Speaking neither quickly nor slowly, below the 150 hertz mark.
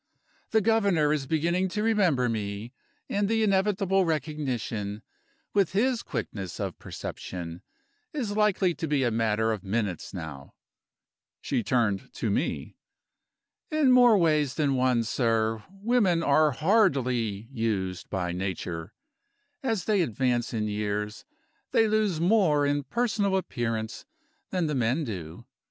No: slow, 130 wpm; medium, 140 Hz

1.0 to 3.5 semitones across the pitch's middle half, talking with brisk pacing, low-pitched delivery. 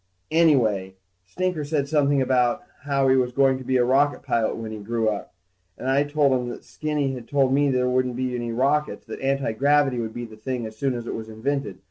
Yes: average, 3.0 semitones; fast, 230 wpm; low, 130 Hz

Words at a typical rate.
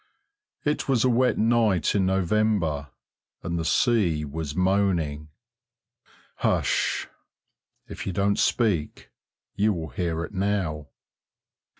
No: slow, 110 wpm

